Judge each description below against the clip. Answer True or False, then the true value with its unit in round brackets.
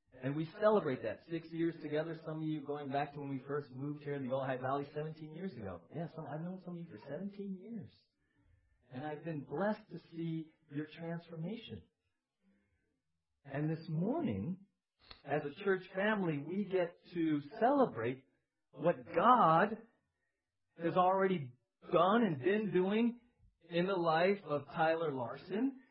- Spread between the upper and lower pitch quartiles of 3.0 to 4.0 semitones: False (4.6 semitones)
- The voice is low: False (160 Hz)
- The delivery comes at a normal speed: True (160 wpm)